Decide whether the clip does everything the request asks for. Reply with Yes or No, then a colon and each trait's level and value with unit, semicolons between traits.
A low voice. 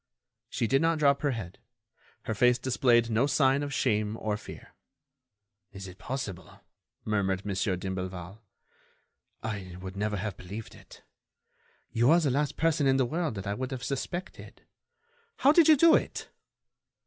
Yes: low, 115 Hz